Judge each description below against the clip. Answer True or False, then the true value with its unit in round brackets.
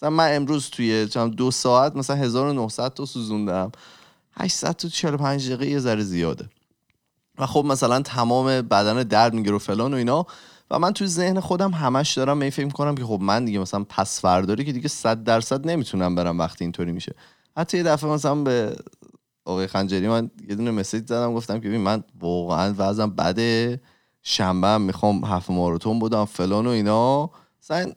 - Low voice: True (115 Hz)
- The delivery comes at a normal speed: False (165 wpm)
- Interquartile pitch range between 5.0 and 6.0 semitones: True (5.6 semitones)